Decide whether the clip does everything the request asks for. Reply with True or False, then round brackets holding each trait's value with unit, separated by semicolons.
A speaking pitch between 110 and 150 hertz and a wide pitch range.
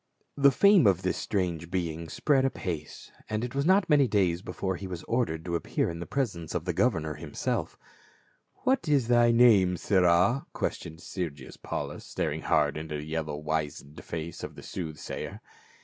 False (90 Hz; 6.9 semitones)